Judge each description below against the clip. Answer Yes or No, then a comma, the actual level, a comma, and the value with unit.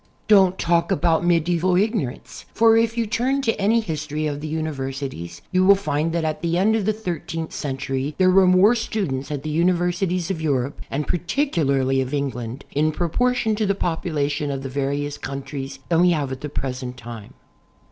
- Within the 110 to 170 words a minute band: No, average, 190 wpm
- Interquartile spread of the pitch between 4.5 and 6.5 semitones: Yes, average, 5.2 semitones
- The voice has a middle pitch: Yes, medium, 160 Hz